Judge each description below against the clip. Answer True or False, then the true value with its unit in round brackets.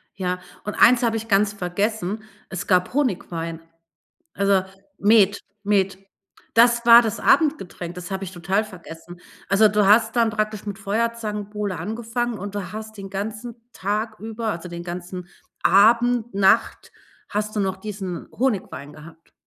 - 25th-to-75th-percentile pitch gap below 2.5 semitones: False (2.9 semitones)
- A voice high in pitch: True (205 Hz)